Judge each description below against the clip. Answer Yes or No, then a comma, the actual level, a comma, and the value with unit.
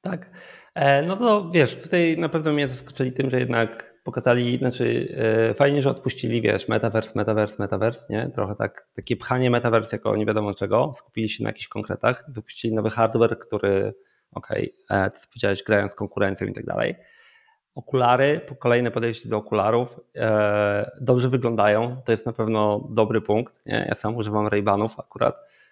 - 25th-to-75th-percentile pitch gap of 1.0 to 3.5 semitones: No, average, 4.1 semitones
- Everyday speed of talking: No, fast, 165 wpm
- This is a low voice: Yes, low, 115 Hz